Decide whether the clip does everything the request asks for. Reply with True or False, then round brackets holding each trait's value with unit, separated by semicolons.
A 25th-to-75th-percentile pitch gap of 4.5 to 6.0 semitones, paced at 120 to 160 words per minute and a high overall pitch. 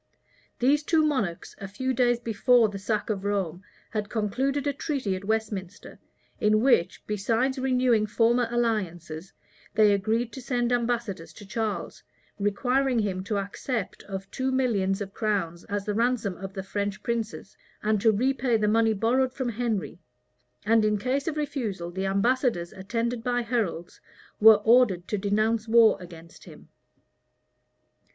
False (3.6 semitones; 150 wpm; 220 Hz)